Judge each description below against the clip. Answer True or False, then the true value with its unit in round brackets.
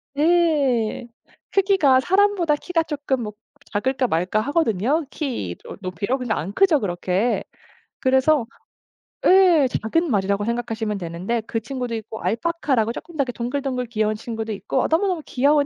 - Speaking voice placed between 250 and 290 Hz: True (255 Hz)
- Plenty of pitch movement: True (5.9 semitones)